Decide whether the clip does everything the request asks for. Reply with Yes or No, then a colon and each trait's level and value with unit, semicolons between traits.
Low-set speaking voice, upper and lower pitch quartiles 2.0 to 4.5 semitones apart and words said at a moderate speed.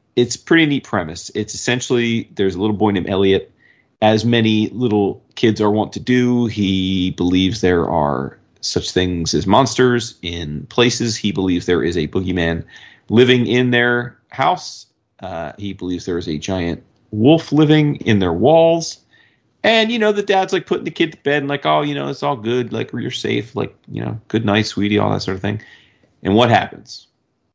No: low, 110 Hz; average, 5.0 semitones; average, 190 wpm